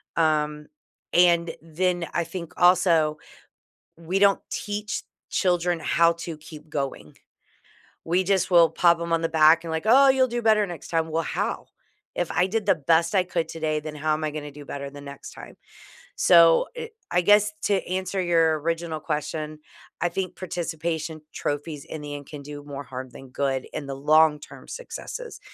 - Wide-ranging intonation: No, average, 2.7 semitones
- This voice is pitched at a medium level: Yes, medium, 165 Hz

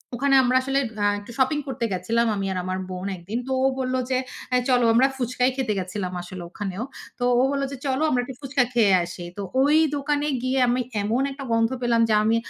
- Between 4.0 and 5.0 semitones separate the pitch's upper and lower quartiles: Yes, average, 4.6 semitones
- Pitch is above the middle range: Yes, high, 245 Hz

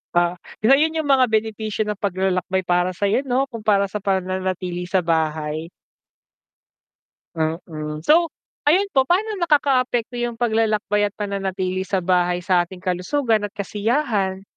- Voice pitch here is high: Yes, high, 200 Hz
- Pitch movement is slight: No, average, 4.7 semitones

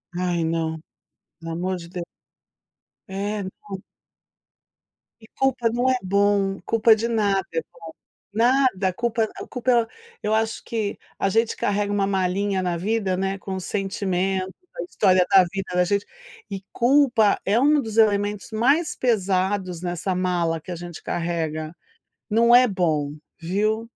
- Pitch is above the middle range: Yes, high, 195 Hz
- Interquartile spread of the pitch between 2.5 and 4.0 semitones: Yes, average, 3.5 semitones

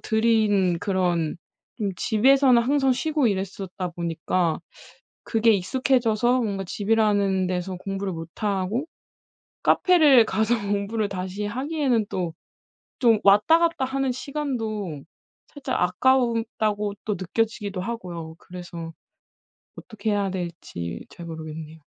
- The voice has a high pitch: Yes, high, 205 Hz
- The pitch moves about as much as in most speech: Yes, average, 4.7 semitones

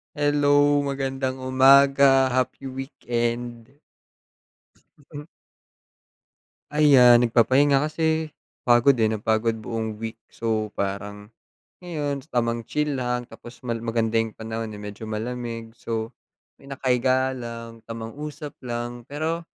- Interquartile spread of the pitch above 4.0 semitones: No, average, 3.4 semitones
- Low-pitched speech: Yes, low, 125 Hz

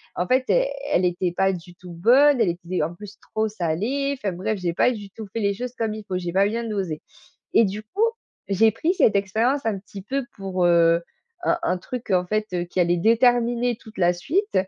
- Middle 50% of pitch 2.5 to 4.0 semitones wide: No, average, 4.7 semitones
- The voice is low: No, high, 205 Hz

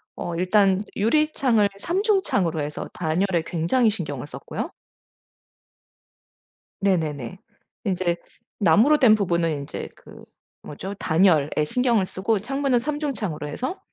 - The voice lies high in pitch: Yes, high, 195 Hz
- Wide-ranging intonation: Yes, wide, 7.0 semitones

